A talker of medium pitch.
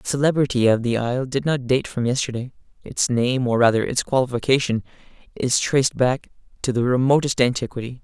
No: low, 125 Hz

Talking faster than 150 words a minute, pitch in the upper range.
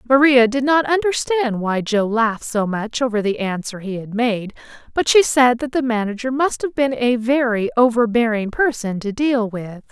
Yes: average, 190 wpm; high, 240 Hz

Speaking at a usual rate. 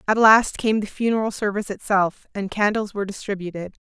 Yes: average, 170 wpm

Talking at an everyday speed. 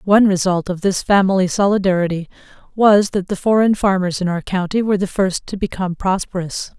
Yes: average, 175 wpm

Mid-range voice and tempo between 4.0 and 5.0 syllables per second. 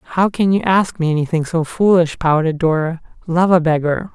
No: medium, 170 Hz; 5.3 syllables/s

